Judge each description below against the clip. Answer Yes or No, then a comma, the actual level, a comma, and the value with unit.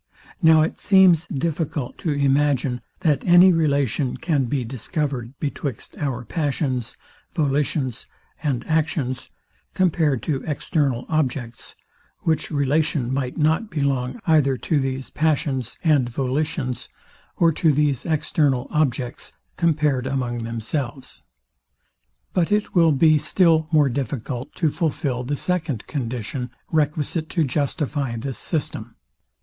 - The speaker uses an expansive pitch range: No, average, 3.6 semitones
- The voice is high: No, medium, 145 Hz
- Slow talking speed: Yes, slow, 120 wpm